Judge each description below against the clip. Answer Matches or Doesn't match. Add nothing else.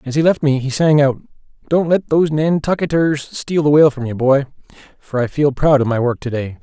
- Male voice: Matches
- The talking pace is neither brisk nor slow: Doesn't match